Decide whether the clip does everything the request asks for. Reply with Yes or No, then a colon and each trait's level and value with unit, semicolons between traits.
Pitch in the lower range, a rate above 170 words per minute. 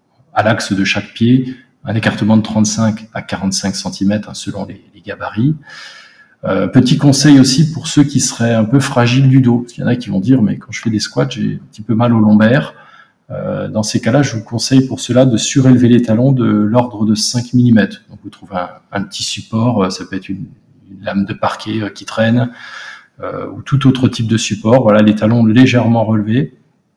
Yes: low, 115 Hz; fast, 220 wpm